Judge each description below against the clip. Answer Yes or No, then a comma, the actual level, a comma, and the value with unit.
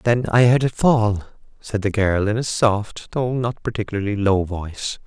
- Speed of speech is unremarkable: Yes, average, 190 wpm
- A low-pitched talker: Yes, low, 110 Hz